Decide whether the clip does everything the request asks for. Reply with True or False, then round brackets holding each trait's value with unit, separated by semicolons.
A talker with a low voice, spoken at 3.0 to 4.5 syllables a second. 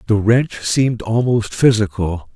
True (110 Hz; 4.2 syllables/s)